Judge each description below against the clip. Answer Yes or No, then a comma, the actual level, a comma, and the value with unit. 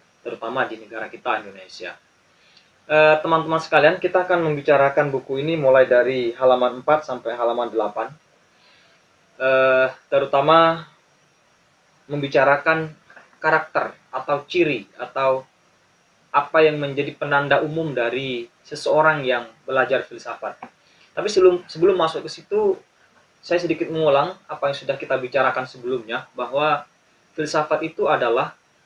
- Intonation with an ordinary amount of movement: Yes, average, 3.7 semitones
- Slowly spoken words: No, average, 110 wpm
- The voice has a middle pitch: Yes, medium, 145 Hz